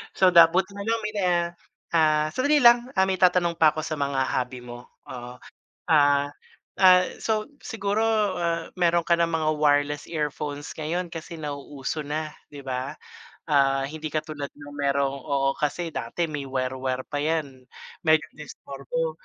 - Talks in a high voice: No, medium, 155 Hz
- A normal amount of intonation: Yes, average, 3.5 semitones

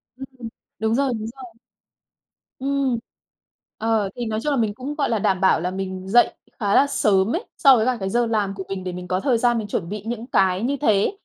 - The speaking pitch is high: Yes, high, 225 Hz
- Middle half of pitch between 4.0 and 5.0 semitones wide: Yes, average, 4.6 semitones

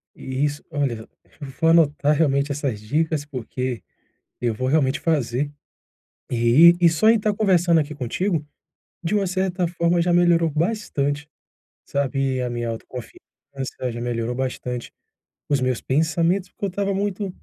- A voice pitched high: No, medium, 145 Hz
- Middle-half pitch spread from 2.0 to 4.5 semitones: No, average, 5.1 semitones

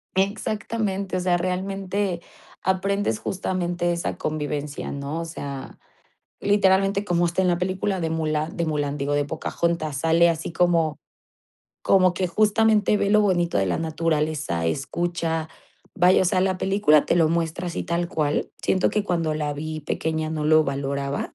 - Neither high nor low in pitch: Yes, medium, 170 Hz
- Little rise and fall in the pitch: No, average, 3.5 semitones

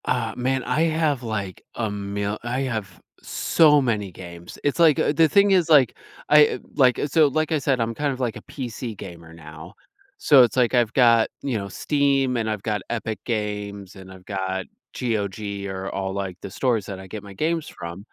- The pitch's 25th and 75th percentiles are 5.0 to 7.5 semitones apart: Yes, wide, 5.5 semitones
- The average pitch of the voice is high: No, low, 115 Hz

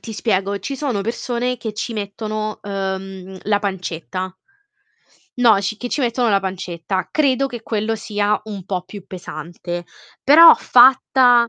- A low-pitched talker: No, high, 210 Hz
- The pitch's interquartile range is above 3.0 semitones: Yes, average, 3.9 semitones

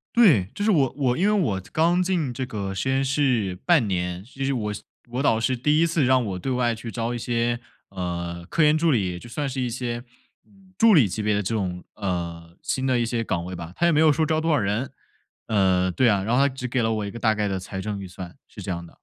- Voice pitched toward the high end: No, low, 115 Hz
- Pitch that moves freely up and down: Yes, wide, 5.9 semitones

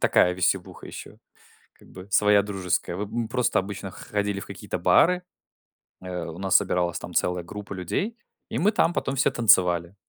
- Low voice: Yes, low, 100 Hz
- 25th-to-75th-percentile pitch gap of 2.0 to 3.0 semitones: No, average, 3.5 semitones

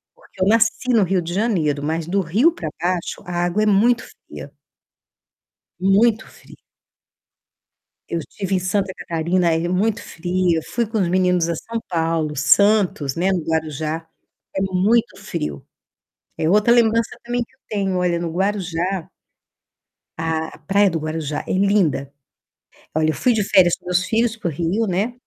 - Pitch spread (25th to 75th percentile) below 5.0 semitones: Yes, average, 4.1 semitones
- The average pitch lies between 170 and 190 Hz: Yes, medium, 185 Hz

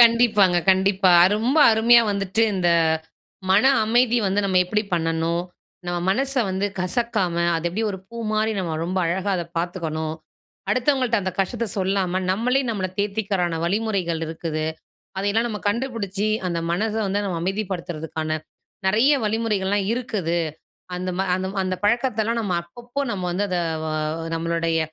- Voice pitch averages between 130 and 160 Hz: No, high, 195 Hz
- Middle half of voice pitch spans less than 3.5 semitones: No, average, 4.0 semitones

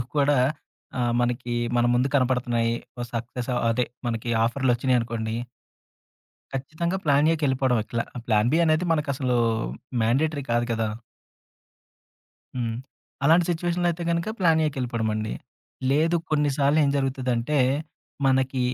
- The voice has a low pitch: Yes, low, 130 Hz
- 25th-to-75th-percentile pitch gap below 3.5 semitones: No, average, 4.0 semitones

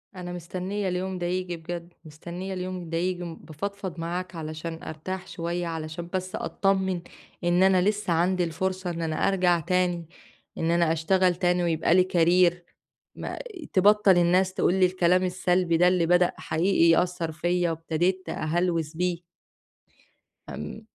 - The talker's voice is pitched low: No, medium, 175 Hz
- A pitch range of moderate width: No, narrow, 1.7 semitones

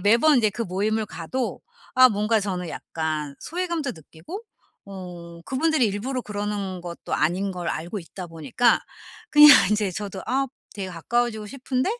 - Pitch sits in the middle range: No, high, 205 Hz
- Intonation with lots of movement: Yes, wide, 5.8 semitones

